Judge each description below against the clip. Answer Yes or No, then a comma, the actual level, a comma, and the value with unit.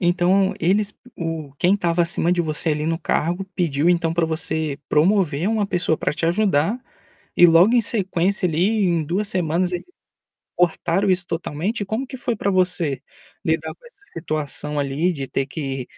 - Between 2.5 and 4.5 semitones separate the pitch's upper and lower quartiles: Yes, average, 3.5 semitones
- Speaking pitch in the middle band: Yes, medium, 175 Hz